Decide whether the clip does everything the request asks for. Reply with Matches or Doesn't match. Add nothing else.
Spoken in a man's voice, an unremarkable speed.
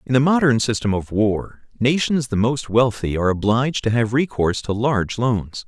Matches